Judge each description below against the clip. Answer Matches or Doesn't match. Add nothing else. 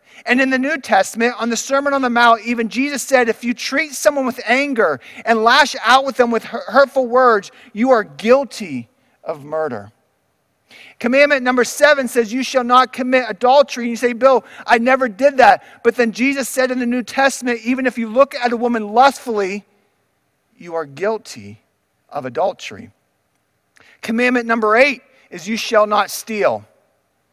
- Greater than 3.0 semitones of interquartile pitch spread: Doesn't match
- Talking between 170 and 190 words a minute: Matches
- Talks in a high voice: Matches